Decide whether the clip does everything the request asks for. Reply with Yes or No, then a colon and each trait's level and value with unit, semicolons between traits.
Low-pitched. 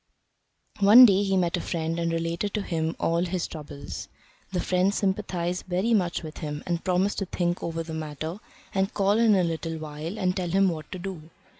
No: medium, 175 Hz